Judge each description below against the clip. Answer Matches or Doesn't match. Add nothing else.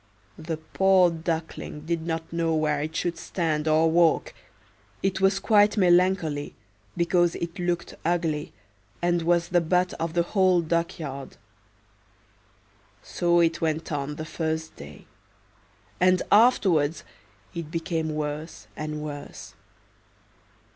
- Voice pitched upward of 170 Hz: Doesn't match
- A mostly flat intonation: Matches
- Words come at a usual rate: Doesn't match